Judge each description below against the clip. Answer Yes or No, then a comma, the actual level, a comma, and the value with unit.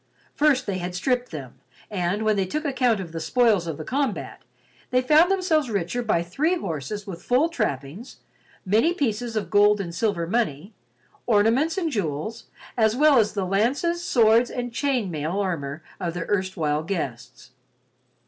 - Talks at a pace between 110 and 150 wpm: No, average, 165 wpm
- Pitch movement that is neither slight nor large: No, wide, 6.4 semitones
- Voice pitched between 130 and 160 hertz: No, high, 210 Hz